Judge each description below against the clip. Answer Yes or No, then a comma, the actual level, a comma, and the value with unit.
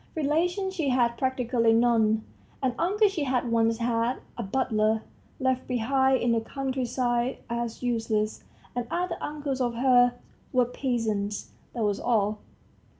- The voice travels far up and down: No, average, 2.8 semitones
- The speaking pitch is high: Yes, high, 245 Hz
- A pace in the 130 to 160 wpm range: Yes, average, 140 wpm